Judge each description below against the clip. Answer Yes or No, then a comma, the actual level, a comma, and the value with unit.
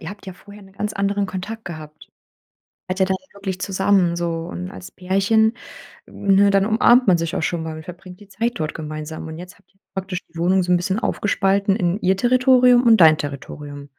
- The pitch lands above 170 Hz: Yes, high, 190 Hz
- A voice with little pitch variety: No, average, 3.3 semitones